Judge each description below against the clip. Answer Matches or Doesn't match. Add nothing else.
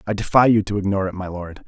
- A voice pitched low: Matches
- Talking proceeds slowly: Doesn't match